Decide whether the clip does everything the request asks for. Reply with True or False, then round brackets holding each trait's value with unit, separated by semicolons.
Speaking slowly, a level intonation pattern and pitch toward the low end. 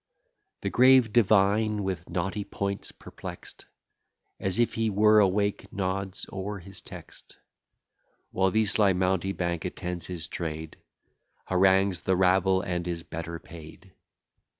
True (125 wpm; 2.3 semitones; 95 Hz)